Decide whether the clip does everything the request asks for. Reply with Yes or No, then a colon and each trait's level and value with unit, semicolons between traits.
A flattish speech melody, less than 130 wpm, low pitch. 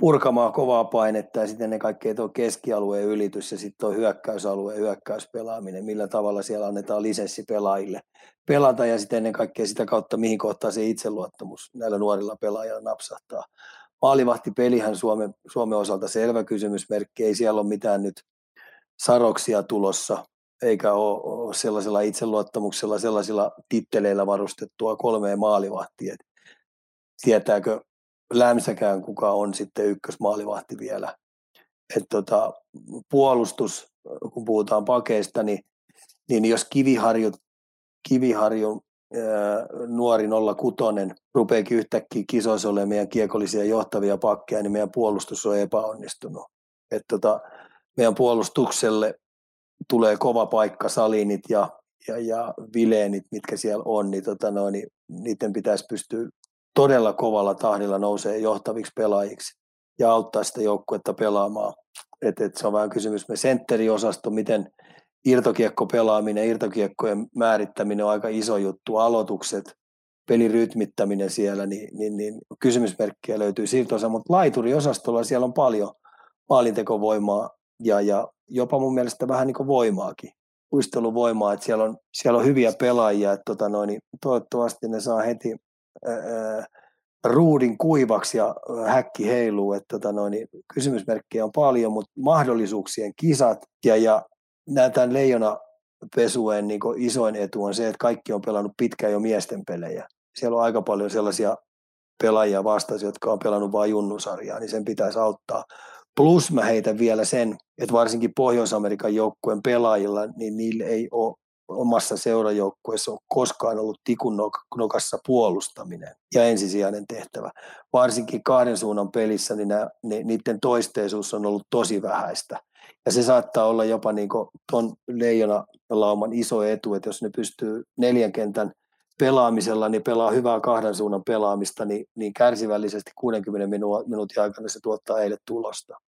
No: narrow, 2.0 semitones; average, 135 wpm; low, 110 Hz